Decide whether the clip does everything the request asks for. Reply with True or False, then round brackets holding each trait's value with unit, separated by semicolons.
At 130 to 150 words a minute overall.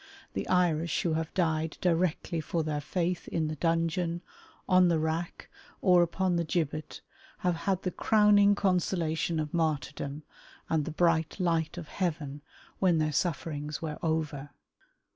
True (145 wpm)